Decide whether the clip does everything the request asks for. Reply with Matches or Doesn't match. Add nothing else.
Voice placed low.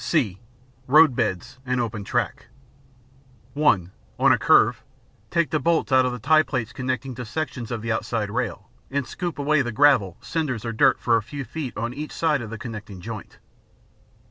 Matches